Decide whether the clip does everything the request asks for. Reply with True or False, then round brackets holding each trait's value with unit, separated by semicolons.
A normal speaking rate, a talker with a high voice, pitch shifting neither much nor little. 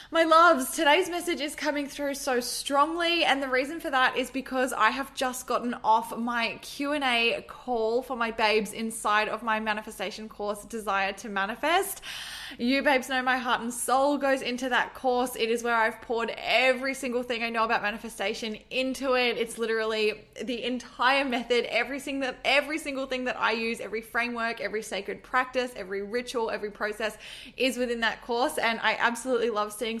True (180 wpm; 240 Hz; 3.0 semitones)